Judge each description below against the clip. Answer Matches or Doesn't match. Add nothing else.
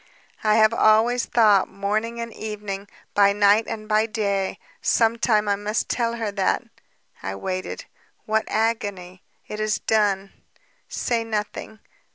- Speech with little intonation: Matches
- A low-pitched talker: Doesn't match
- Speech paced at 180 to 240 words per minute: Doesn't match